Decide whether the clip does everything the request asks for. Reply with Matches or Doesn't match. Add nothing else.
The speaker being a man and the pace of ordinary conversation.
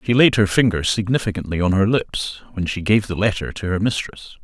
Doesn't match